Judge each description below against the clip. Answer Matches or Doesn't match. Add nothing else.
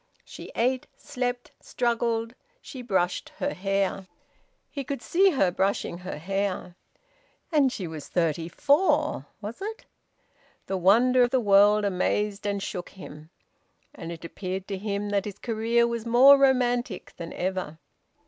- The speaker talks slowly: Doesn't match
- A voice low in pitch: Doesn't match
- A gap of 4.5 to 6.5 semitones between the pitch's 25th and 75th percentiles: Matches